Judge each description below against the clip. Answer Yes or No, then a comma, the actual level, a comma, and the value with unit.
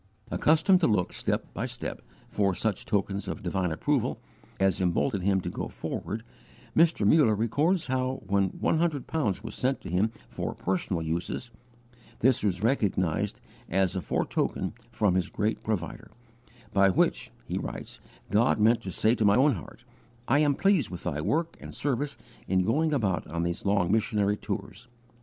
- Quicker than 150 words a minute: Yes, average, 170 wpm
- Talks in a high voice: No, low, 105 Hz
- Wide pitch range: Yes, wide, 5.8 semitones